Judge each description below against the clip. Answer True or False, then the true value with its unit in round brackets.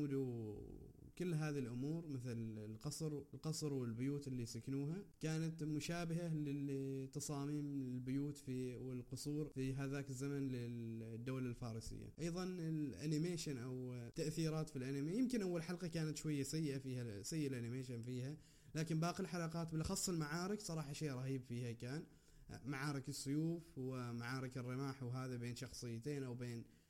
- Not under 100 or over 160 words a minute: True (125 wpm)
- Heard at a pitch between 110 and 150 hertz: True (140 Hz)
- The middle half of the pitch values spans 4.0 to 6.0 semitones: False (3.6 semitones)